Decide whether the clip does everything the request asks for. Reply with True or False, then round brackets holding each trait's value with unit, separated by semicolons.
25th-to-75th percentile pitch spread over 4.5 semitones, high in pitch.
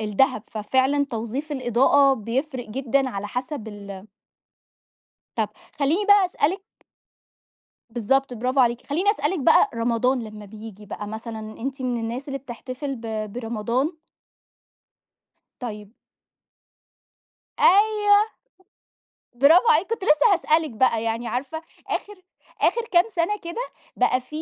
True (5.2 semitones; 255 Hz)